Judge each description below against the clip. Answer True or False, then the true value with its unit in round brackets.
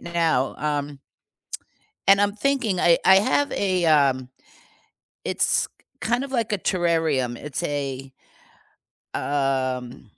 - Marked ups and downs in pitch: True (6.5 semitones)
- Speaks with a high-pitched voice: False (160 Hz)